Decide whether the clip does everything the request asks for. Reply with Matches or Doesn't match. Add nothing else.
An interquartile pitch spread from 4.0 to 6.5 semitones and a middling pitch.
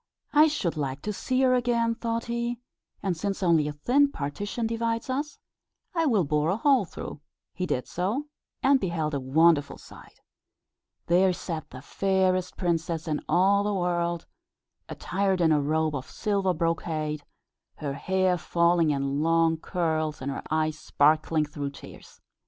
Matches